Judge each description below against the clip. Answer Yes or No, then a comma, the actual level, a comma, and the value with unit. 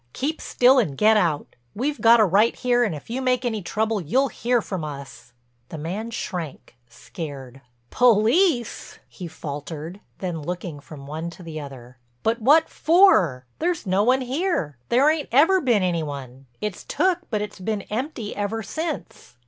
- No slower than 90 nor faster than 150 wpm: No, average, 165 wpm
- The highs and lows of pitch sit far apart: Yes, wide, 7.9 semitones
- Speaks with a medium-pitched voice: No, high, 210 Hz